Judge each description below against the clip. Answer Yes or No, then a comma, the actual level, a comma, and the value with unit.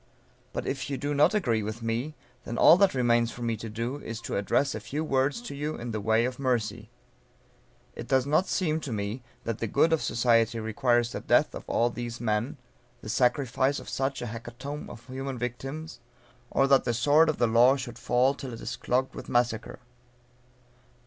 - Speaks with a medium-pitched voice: No, low, 125 Hz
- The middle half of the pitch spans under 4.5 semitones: Yes, average, 3.2 semitones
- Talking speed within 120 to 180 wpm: No, average, 200 wpm